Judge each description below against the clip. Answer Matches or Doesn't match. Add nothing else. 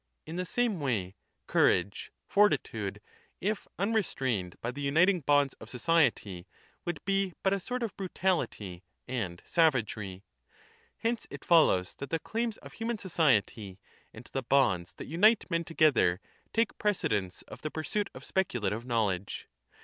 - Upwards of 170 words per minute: Doesn't match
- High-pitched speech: Doesn't match